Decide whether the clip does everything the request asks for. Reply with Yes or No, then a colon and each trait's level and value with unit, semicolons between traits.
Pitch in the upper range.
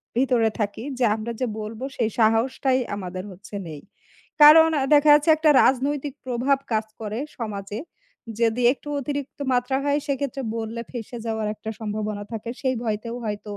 Yes: high, 235 Hz